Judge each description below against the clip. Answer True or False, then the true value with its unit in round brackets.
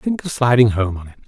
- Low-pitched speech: True (125 Hz)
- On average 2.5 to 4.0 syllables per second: False (6.0 syllables/s)